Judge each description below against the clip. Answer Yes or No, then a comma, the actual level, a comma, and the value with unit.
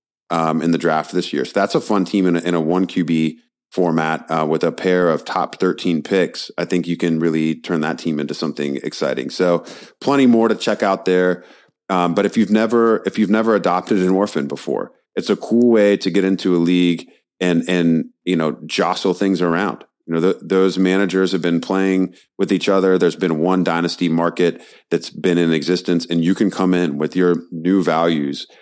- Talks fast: Yes, fast, 210 wpm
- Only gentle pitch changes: Yes, narrow, 2.3 semitones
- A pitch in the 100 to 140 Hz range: No, very low, 90 Hz